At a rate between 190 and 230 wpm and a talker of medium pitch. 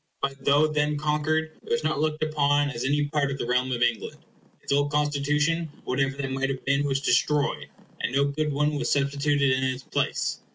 Yes: fast, 205 wpm; medium, 145 Hz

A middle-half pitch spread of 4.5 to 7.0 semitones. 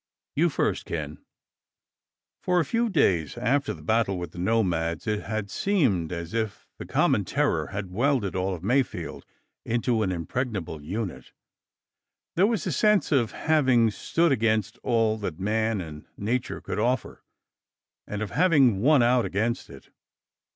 Yes: wide, 5.4 semitones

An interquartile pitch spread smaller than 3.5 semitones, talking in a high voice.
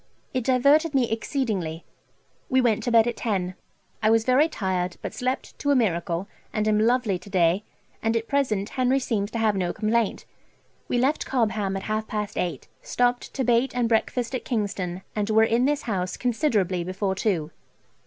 No: average, 4.3 semitones; high, 220 Hz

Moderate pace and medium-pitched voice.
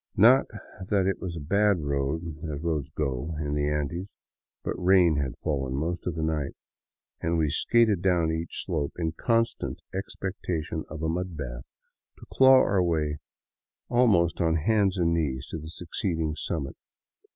No: average, 160 wpm; very low, 80 Hz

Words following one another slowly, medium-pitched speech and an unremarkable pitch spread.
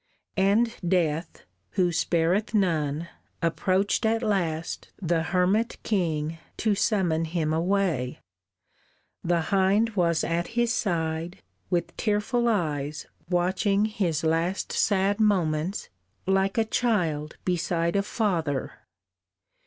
Yes: slow, 105 wpm; medium, 180 Hz; average, 3.8 semitones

